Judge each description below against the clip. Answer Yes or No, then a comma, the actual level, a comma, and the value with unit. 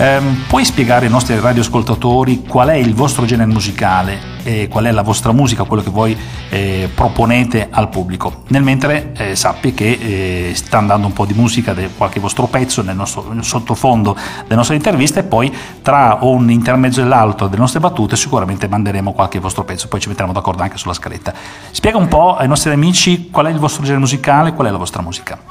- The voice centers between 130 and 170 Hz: No, low, 115 Hz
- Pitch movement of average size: Yes, average, 4.5 semitones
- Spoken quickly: Yes, fast, 195 wpm